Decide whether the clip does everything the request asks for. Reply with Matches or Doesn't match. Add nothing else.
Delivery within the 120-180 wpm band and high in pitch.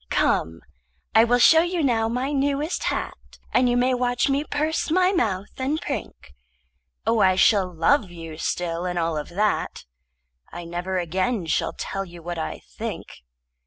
Matches